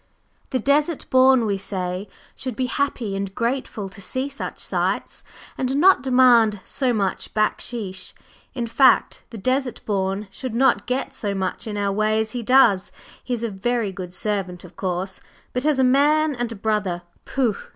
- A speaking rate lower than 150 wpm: No, average, 175 wpm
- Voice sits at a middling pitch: No, high, 225 Hz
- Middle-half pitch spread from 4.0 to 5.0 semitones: Yes, average, 4.7 semitones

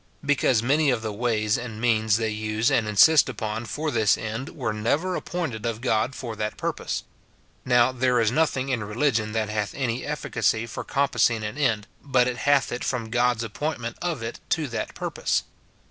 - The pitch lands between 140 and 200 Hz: No, low, 120 Hz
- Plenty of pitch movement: No, average, 3.3 semitones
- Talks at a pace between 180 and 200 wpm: Yes, average, 185 wpm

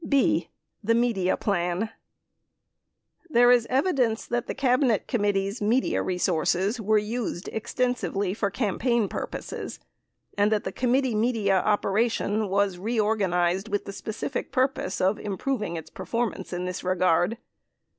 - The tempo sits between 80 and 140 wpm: Yes, slow, 135 wpm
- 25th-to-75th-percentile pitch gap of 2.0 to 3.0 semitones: No, average, 3.8 semitones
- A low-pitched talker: No, high, 210 Hz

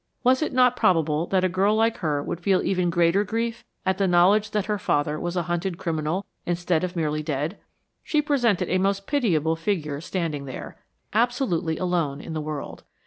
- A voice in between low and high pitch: Yes, medium, 180 Hz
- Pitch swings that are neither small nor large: Yes, average, 4.3 semitones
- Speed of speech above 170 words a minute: Yes, average, 190 wpm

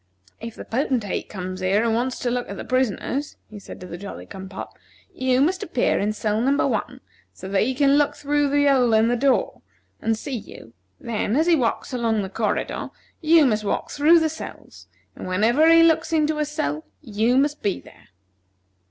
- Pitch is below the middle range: No, high, 245 Hz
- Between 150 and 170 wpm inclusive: No, fast, 205 wpm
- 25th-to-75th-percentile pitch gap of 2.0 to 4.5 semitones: No, wide, 5.5 semitones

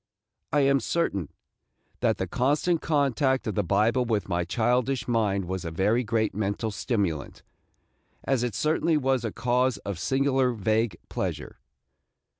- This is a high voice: No, low, 115 Hz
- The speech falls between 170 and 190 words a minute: No, average, 150 wpm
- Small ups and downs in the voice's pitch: No, average, 4.7 semitones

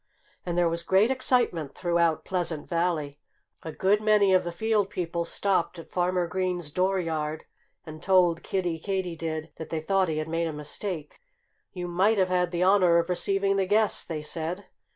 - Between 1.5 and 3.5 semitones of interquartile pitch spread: Yes, average, 2.7 semitones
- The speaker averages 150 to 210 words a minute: Yes, average, 175 wpm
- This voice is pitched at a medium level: Yes, medium, 175 Hz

